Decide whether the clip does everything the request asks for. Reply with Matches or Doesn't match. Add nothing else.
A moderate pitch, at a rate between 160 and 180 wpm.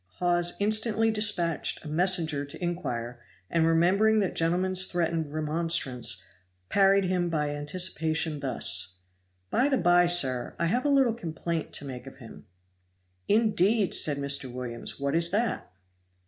Doesn't match